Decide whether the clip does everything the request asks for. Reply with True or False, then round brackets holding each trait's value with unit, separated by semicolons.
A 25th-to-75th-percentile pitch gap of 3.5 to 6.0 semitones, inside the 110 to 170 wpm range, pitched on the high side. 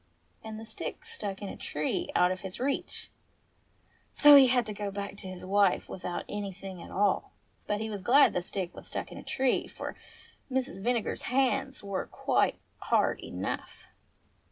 False (4.4 semitones; 180 wpm; 205 Hz)